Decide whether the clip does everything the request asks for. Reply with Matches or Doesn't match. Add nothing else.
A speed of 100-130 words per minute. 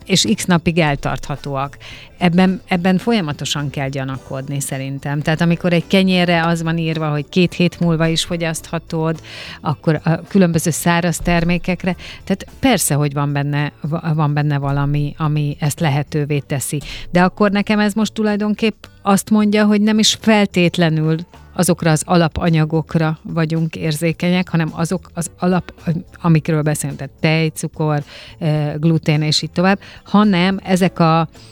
Doesn't match